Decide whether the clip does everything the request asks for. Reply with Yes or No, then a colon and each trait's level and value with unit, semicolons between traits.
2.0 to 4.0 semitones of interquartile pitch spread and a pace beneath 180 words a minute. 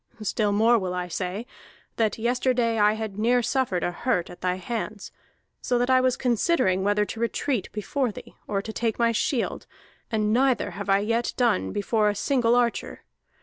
No: average, 3.1 semitones; average, 185 wpm